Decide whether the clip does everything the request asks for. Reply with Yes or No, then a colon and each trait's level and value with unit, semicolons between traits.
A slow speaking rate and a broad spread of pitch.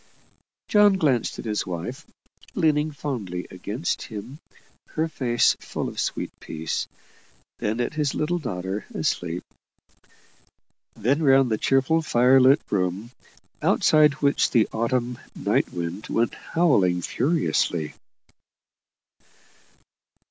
Yes: slow, 110 wpm; wide, 6.9 semitones